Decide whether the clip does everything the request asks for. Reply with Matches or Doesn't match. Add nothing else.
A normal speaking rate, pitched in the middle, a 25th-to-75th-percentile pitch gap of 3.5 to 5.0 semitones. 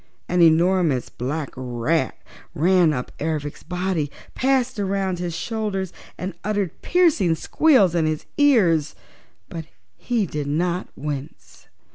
Doesn't match